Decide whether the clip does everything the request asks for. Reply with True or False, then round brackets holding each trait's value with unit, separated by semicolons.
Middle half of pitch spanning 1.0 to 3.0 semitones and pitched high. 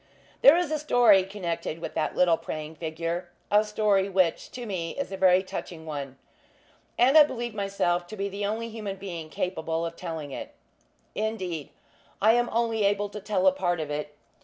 False (4.6 semitones; 195 Hz)